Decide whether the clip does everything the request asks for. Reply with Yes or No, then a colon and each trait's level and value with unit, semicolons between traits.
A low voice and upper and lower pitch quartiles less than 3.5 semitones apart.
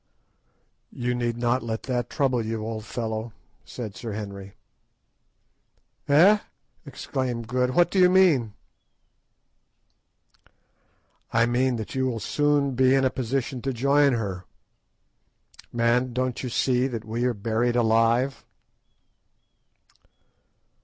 Yes: low, 120 Hz; narrow, 2.5 semitones